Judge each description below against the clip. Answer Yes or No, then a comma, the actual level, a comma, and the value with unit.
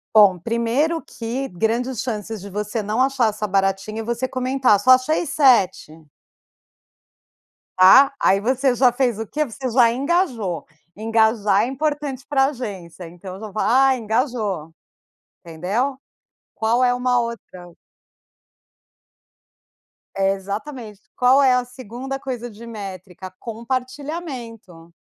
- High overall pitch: Yes, high, 230 Hz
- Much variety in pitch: No, average, 4.4 semitones